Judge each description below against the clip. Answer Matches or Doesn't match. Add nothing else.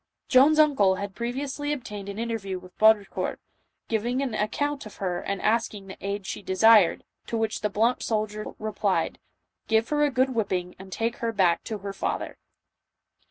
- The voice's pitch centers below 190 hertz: Doesn't match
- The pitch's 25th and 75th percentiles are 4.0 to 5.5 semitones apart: Doesn't match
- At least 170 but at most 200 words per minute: Matches